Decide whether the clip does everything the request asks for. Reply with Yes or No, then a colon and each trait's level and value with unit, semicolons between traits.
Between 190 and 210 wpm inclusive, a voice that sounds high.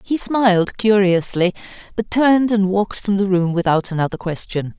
No: average, 165 wpm; high, 195 Hz